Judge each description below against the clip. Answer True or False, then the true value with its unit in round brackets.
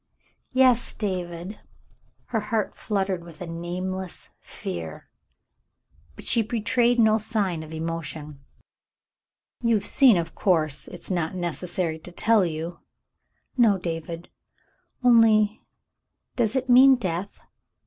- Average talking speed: False (120 wpm)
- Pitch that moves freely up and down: False (5.0 semitones)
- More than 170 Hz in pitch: True (185 Hz)